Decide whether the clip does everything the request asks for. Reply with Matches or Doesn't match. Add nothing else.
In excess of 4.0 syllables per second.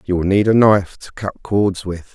Matches